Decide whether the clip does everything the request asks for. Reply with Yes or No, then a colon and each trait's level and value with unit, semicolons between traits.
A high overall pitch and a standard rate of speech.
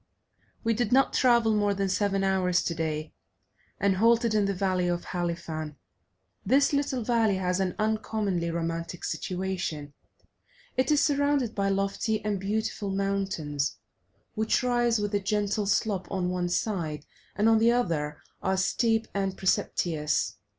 Yes: high, 195 Hz; average, 145 wpm